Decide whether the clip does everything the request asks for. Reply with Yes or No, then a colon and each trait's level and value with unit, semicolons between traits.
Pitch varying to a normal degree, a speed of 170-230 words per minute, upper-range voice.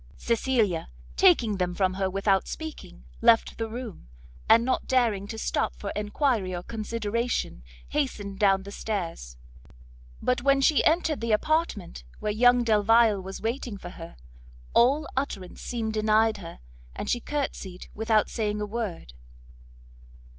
No: average, 3.8 semitones; average, 140 wpm; high, 220 Hz